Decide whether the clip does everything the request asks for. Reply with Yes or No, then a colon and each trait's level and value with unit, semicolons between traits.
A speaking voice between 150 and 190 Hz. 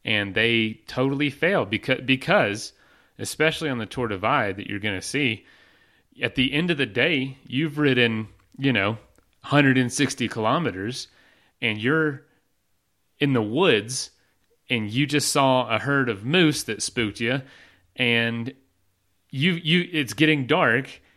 No: low, 125 Hz